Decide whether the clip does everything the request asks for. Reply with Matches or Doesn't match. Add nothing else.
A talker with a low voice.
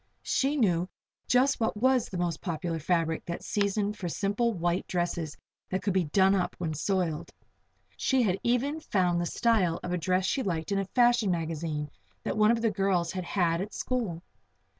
Doesn't match